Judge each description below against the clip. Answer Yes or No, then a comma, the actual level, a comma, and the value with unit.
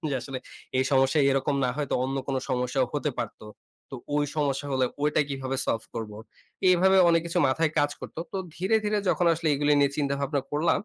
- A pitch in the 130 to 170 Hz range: Yes, medium, 140 Hz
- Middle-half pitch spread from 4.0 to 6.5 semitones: No, narrow, 2.6 semitones